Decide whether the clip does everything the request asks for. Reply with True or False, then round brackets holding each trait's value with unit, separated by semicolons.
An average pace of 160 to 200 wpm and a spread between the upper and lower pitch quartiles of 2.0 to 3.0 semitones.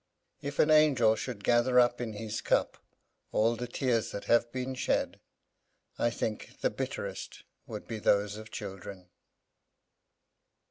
False (140 wpm; 2.6 semitones)